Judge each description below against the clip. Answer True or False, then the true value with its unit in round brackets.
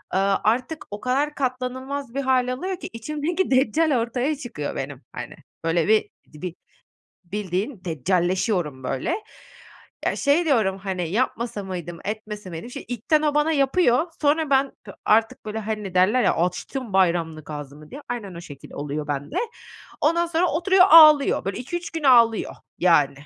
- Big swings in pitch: True (7.7 semitones)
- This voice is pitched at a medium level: False (225 Hz)